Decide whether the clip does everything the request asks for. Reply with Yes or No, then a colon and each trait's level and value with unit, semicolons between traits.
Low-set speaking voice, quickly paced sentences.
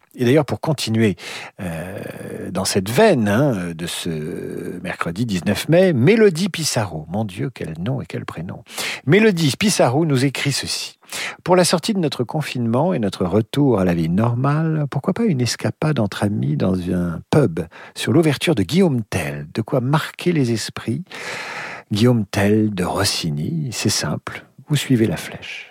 No: low, 125 Hz; average, 165 wpm